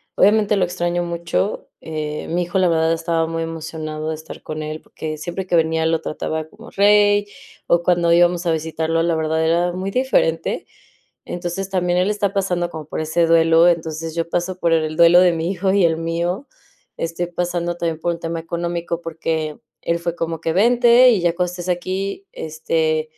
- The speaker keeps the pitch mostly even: Yes, narrow, 1.7 semitones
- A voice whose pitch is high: No, medium, 170 Hz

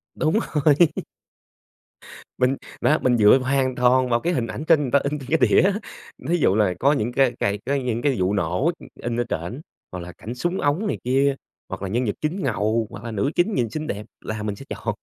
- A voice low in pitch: Yes, low, 125 Hz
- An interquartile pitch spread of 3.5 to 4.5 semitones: No, average, 5.2 semitones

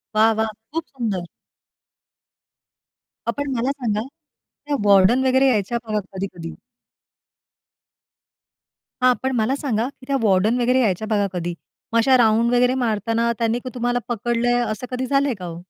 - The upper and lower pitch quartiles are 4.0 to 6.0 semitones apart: No, average, 3.1 semitones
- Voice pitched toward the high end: Yes, high, 235 Hz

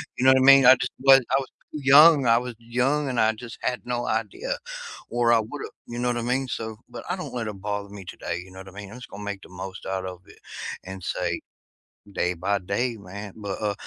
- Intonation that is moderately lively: Yes, average, 4.2 semitones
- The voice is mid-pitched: No, low, 115 Hz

